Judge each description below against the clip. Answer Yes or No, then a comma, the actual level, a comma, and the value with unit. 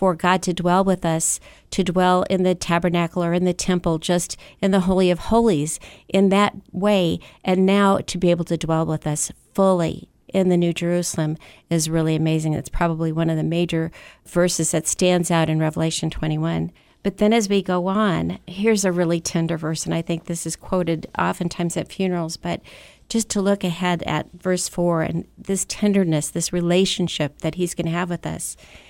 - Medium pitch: Yes, medium, 175 Hz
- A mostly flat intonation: Yes, narrow, 2.3 semitones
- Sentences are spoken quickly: No, average, 195 wpm